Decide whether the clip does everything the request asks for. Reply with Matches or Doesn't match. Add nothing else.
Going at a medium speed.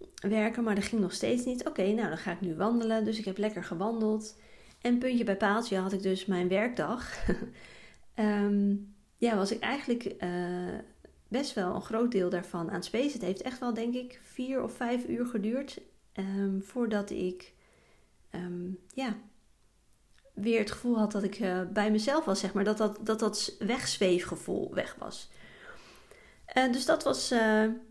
Matches